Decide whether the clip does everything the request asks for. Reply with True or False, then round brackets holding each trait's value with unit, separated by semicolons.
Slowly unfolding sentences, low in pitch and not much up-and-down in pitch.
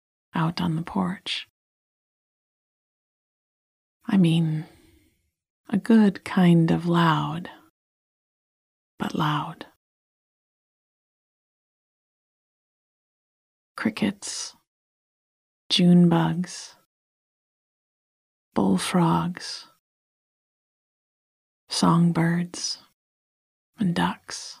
False (50 wpm; 170 Hz; 2.0 semitones)